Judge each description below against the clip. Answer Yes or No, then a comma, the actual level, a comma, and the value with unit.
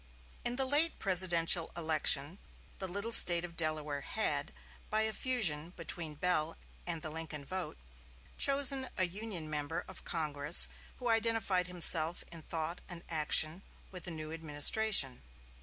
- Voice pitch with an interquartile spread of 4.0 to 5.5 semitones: Yes, average, 4.3 semitones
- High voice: No, medium, 170 Hz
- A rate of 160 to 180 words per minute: No, average, 145 wpm